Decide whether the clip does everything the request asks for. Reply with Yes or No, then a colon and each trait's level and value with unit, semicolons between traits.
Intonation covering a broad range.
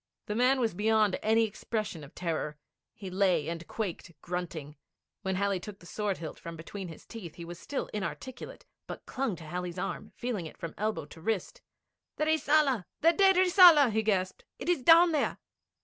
Yes: wide, 6.5 semitones